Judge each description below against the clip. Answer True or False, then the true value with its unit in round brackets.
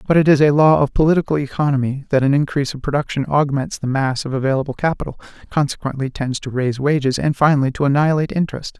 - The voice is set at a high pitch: False (140 Hz)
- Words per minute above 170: True (200 wpm)